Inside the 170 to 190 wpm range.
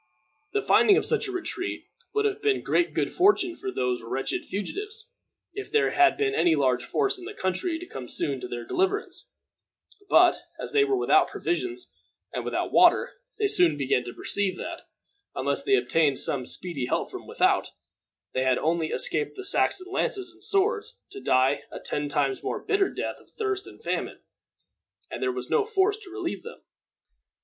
Yes: average, 185 wpm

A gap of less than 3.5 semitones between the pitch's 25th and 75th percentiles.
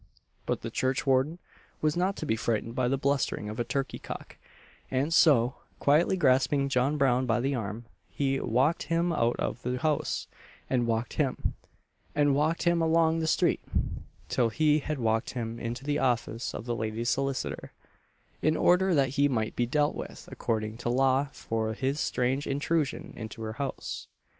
No: average, 3.8 semitones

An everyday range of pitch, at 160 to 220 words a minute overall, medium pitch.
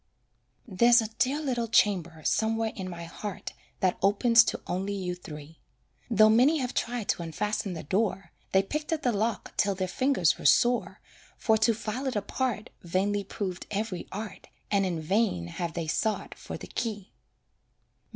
No: average, 3.9 semitones; average, 170 wpm; high, 205 Hz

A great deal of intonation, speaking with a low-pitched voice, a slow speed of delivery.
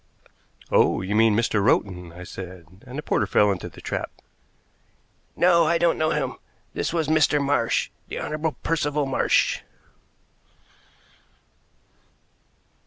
Yes: wide, 8.1 semitones; low, 130 Hz; slow, 125 wpm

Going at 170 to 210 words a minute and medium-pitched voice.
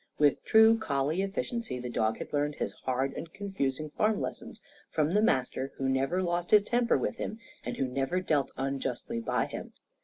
Yes: average, 185 wpm; medium, 150 Hz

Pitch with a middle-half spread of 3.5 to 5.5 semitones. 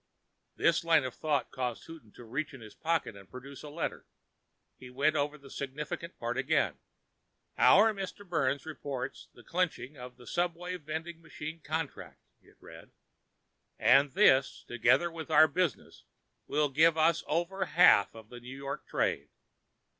Yes: average, 4.1 semitones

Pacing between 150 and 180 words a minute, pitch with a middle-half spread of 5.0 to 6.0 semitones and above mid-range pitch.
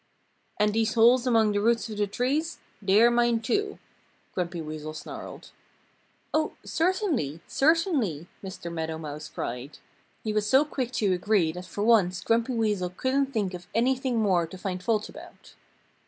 Yes: average, 160 wpm; wide, 5.6 semitones; high, 215 Hz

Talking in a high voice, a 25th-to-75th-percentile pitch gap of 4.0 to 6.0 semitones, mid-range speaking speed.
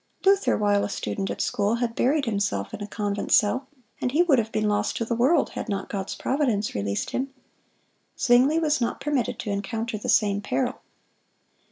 Yes: high, 225 Hz; average, 4.3 semitones; average, 190 wpm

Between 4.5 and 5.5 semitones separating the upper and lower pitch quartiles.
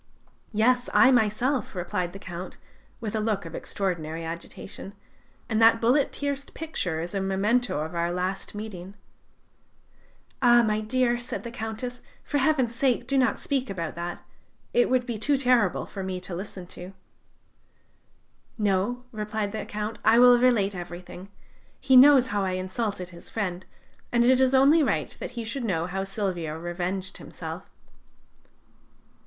Yes: average, 5.0 semitones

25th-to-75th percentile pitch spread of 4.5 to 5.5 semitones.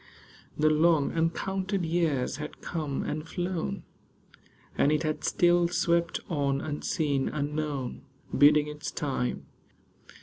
No: average, 2.7 semitones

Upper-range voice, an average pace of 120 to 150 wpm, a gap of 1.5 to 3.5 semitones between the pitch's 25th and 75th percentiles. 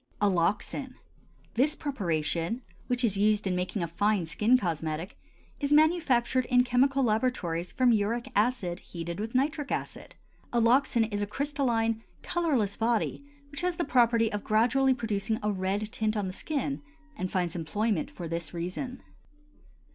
No: high, 225 Hz; average, 145 wpm; average, 5.3 semitones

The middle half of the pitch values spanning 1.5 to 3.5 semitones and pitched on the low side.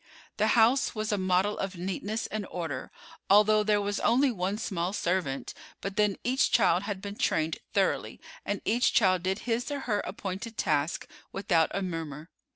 No: average, 3.1 semitones; high, 200 Hz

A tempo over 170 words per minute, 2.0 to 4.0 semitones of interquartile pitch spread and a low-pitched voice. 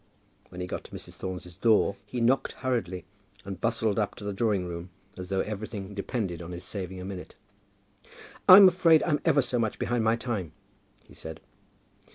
No: average, 185 wpm; average, 4.6 semitones; low, 100 Hz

